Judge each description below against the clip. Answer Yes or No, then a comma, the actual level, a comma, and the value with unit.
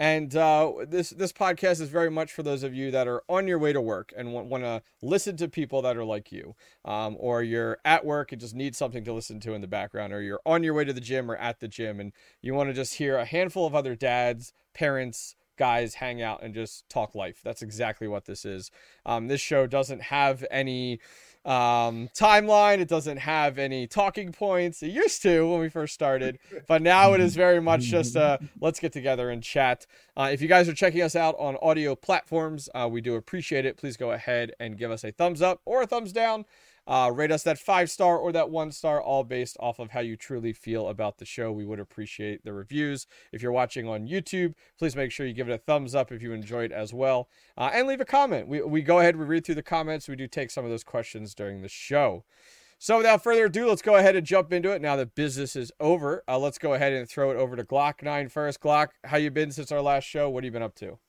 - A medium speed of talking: No, fast, 250 wpm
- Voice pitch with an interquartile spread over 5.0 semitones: Yes, wide, 5.5 semitones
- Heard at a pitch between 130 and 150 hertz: Yes, medium, 140 Hz